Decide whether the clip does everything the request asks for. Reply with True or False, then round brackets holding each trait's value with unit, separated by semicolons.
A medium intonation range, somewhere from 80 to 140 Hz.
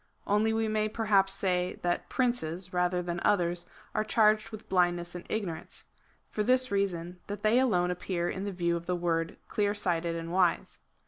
False (3.4 semitones; 185 Hz)